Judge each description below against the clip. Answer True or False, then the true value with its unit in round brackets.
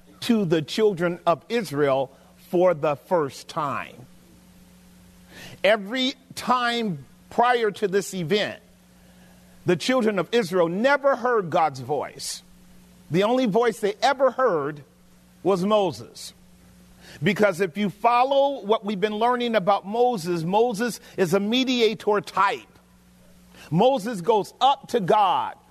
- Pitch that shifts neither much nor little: False (8.6 semitones)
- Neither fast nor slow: False (120 wpm)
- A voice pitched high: True (200 Hz)